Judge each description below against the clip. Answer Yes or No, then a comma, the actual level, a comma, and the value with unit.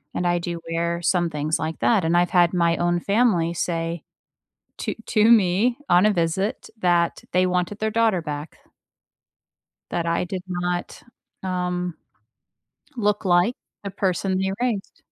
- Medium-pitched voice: Yes, medium, 180 Hz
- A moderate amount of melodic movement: No, narrow, 2.3 semitones